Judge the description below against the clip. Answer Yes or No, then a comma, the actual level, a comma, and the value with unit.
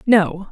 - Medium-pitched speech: No, high, 205 Hz